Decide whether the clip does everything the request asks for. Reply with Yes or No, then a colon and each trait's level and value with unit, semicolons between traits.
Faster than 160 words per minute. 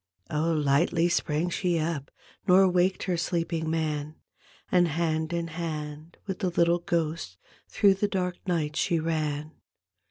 No: average, 145 wpm